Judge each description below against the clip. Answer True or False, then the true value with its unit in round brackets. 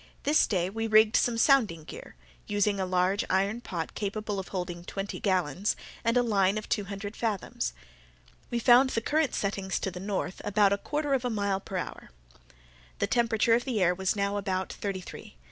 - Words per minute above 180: True (195 wpm)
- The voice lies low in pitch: False (200 Hz)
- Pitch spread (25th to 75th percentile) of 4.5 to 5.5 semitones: False (3.1 semitones)